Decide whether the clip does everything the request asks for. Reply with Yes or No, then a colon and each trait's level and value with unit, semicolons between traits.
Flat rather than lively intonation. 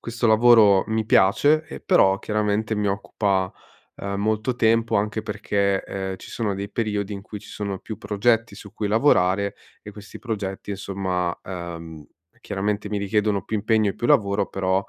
Yes: narrow, 2.0 semitones